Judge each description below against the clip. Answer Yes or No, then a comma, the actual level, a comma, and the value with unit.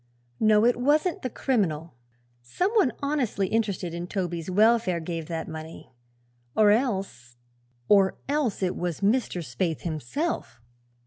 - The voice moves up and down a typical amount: No, wide, 6.4 semitones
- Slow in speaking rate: Yes, slow, 130 wpm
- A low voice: No, high, 195 Hz